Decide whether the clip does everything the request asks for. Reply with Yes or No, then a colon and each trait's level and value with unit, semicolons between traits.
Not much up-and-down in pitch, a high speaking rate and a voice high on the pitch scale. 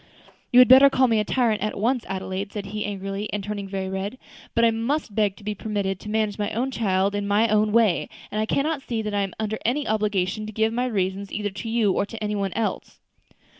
Yes: narrow, 2.2 semitones; fast, 245 wpm; high, 210 Hz